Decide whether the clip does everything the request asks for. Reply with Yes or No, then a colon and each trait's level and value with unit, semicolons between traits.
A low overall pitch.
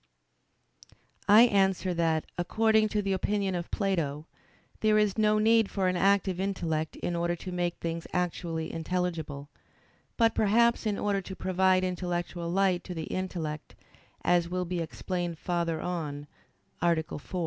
No: medium, 180 Hz